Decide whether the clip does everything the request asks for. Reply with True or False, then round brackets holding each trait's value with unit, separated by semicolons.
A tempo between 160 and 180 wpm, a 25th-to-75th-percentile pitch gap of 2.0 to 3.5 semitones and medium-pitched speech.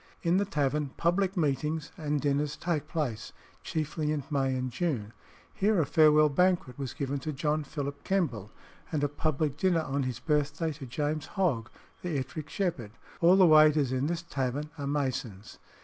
True (170 wpm; 2.9 semitones; 150 Hz)